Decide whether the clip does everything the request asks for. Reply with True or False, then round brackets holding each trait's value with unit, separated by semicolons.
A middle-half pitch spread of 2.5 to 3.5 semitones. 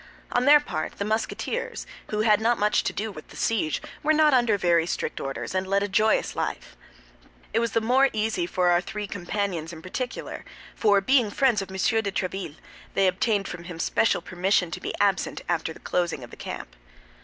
False (4.0 semitones)